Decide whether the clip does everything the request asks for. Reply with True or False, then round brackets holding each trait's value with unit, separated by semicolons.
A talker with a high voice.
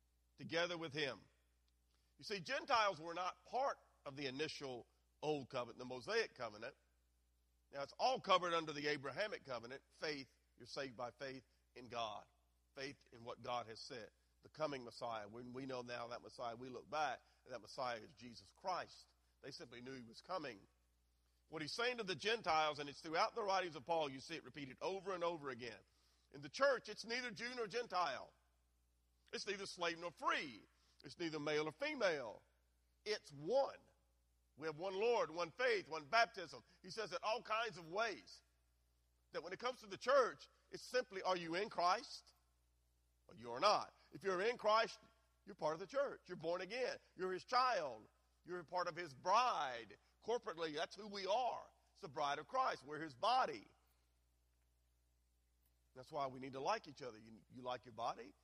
False (140 Hz)